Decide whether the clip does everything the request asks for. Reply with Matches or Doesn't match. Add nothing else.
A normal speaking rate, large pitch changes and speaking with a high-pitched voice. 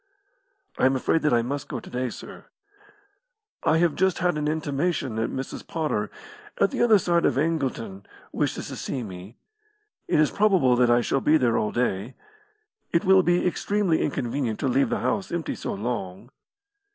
Doesn't match